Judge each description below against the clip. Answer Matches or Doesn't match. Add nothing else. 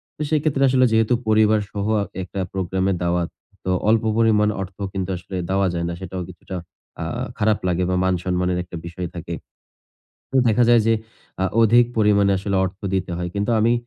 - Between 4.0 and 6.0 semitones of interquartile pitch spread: Doesn't match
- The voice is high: Doesn't match